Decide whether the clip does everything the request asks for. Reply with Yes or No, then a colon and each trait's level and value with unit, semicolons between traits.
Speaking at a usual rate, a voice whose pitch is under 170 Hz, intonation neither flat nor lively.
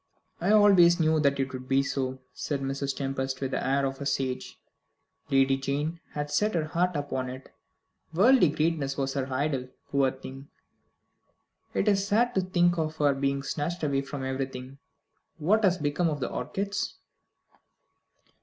Yes: average, 165 wpm; medium, 140 Hz; average, 4.1 semitones